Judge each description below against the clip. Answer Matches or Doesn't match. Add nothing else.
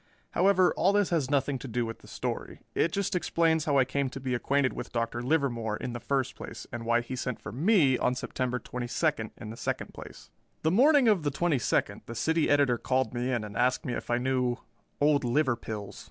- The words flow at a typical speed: Doesn't match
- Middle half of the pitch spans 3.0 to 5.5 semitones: Matches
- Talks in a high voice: Doesn't match